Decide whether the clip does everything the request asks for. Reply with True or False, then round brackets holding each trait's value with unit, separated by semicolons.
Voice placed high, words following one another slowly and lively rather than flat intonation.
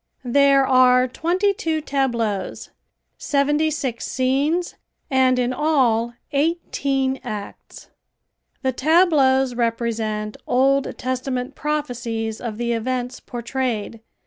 False (260 Hz; 95 wpm; 3.0 semitones)